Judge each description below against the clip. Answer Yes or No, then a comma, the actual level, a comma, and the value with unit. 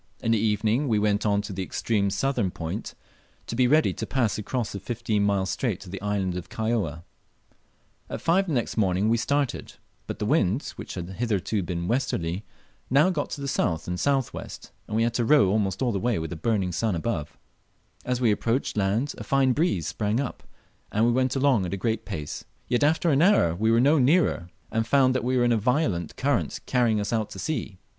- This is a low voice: Yes, low, 110 Hz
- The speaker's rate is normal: No, fast, 215 wpm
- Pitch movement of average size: Yes, average, 4.8 semitones